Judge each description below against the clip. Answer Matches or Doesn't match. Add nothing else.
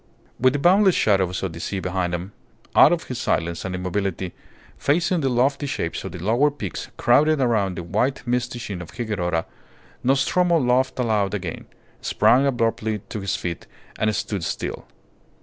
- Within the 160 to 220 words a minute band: Matches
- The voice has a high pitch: Doesn't match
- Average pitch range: Doesn't match